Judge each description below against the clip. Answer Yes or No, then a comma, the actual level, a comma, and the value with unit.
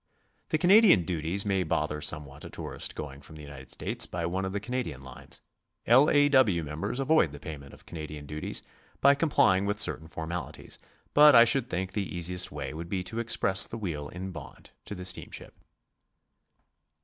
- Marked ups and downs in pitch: Yes, wide, 6.7 semitones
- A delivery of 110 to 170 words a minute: No, average, 185 wpm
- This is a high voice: No, very low, 90 Hz